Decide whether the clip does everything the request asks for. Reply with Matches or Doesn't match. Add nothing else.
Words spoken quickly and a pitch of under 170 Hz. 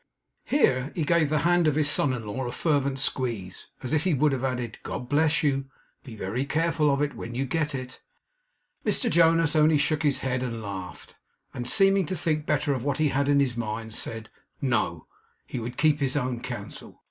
Matches